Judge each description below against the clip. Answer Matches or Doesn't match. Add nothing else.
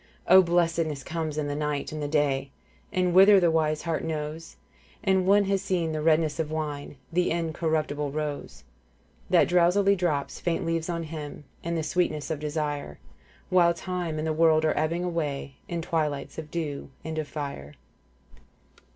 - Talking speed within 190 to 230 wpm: Matches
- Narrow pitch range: Matches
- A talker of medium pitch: Matches